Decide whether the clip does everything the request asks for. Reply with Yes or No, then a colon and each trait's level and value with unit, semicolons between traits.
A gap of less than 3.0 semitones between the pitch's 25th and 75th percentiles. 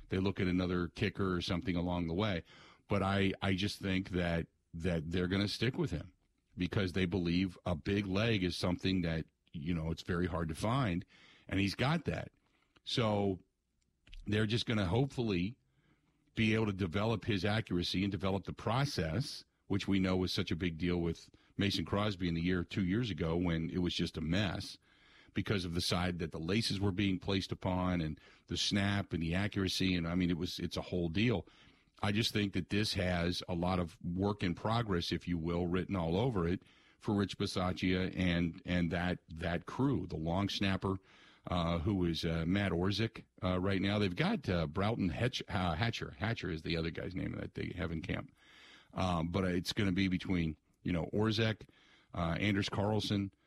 Yes: narrow, 2.6 semitones